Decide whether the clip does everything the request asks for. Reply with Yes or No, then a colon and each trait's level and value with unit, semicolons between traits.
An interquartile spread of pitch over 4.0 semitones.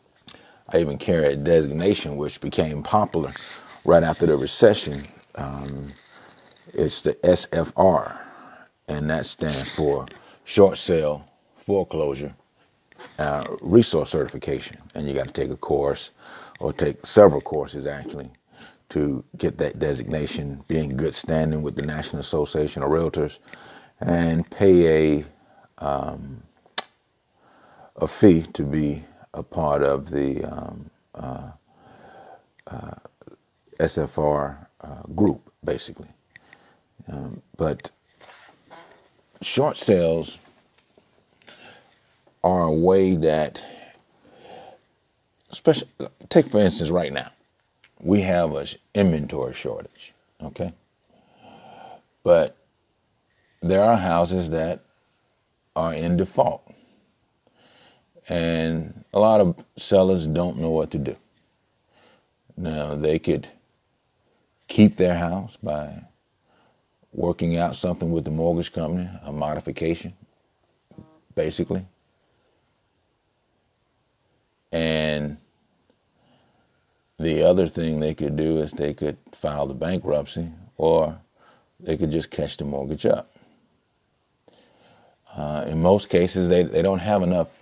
No: average, 2.9 semitones